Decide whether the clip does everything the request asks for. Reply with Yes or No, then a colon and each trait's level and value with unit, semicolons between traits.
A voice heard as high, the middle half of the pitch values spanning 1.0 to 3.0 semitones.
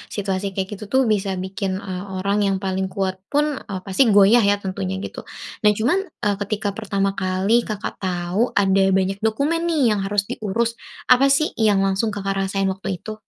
Yes: high, 200 Hz; narrow, 2.4 semitones